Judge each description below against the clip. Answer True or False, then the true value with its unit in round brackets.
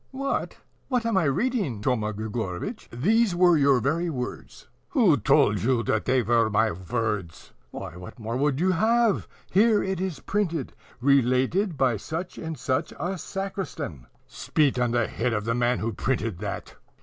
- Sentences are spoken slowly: False (165 wpm)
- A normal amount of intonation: False (8.4 semitones)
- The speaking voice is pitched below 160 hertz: True (135 Hz)